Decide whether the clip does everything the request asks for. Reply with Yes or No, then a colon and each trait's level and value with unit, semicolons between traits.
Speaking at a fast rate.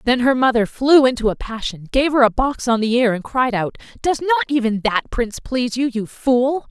Yes: fast, 235 wpm